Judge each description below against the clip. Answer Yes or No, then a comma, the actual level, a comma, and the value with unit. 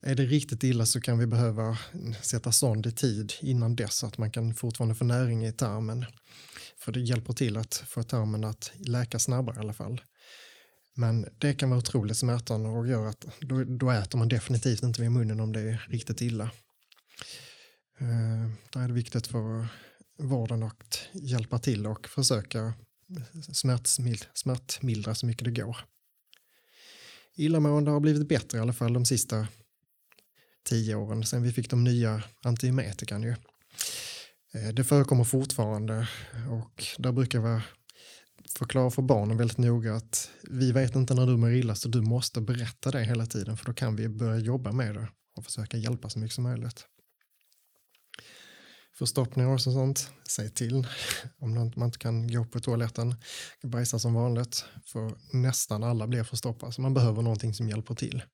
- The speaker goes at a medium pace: Yes, average, 170 wpm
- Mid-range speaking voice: No, low, 120 Hz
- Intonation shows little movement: Yes, narrow, 2.1 semitones